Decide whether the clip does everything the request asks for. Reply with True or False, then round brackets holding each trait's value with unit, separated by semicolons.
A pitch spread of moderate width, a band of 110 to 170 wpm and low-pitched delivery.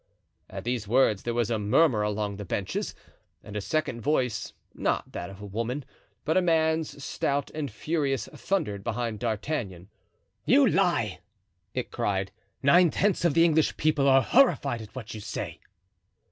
False (6.7 semitones; 160 wpm; 125 Hz)